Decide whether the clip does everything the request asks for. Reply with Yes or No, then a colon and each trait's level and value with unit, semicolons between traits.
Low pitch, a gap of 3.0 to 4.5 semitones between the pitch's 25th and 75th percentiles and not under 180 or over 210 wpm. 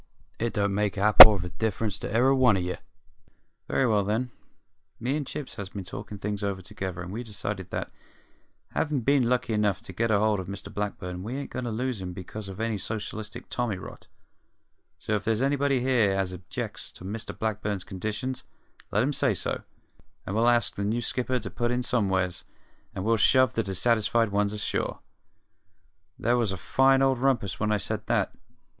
Yes: low, 110 Hz; average, 3.6 semitones; average, 195 wpm